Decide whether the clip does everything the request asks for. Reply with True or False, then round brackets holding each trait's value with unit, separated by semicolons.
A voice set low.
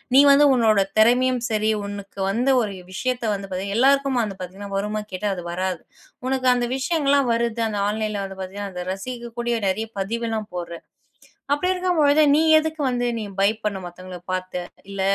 False (215 Hz)